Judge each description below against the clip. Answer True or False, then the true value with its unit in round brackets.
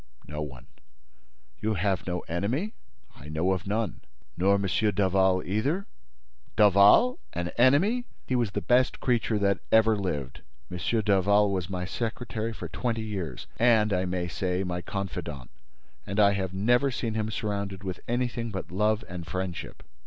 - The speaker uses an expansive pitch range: False (3.6 semitones)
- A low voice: True (100 Hz)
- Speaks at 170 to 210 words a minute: False (155 wpm)